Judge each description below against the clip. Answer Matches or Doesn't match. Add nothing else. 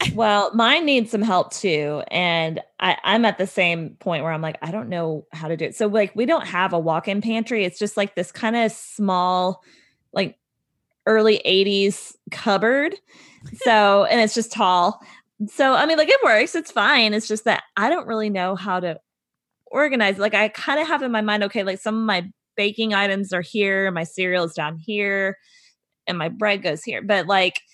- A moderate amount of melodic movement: Matches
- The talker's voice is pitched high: Matches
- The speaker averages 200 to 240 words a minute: Matches